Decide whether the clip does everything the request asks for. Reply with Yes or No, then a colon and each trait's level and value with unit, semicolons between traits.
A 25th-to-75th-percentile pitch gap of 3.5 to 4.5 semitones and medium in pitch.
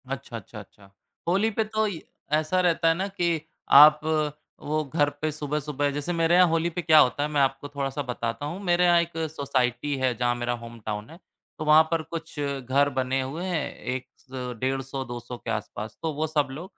Yes: average, 4.0 semitones; medium, 145 Hz